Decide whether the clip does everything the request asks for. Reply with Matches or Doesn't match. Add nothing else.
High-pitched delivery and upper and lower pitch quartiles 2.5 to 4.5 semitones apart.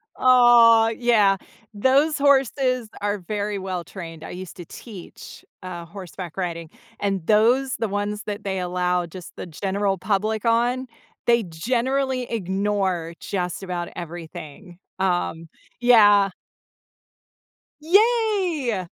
Doesn't match